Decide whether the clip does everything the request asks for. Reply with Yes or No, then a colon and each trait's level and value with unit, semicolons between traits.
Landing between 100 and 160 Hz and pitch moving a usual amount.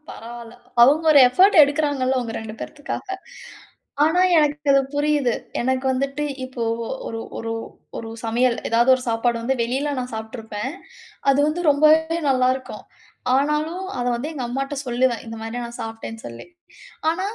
No: very high, 260 Hz; average, 4.0 semitones